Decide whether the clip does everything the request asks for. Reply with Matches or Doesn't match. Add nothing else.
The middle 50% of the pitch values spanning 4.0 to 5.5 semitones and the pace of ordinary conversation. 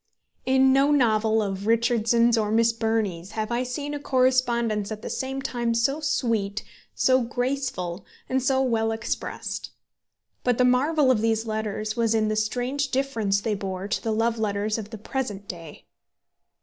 Doesn't match